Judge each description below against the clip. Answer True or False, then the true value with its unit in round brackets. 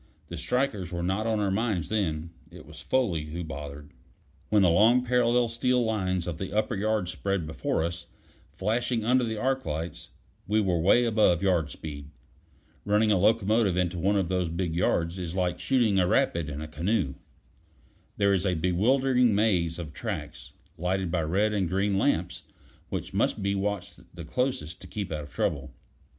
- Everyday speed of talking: True (180 wpm)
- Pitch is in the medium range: False (95 Hz)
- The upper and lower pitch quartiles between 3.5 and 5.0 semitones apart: True (4.3 semitones)